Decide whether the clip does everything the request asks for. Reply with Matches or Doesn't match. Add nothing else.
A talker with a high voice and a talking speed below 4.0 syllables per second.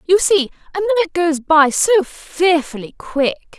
Doesn't match